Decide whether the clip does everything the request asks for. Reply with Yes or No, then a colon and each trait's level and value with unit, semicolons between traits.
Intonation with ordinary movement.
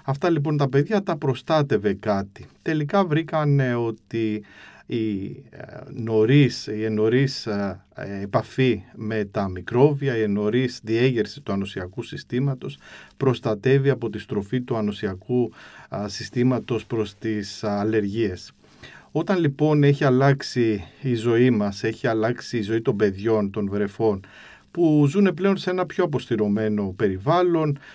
Yes: average, 4.7 semitones